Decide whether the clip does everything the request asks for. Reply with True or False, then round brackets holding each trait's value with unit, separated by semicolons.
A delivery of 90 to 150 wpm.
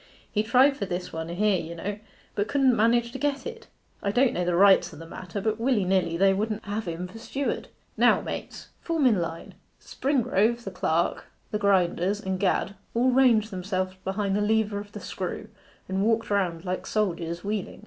False (195 wpm)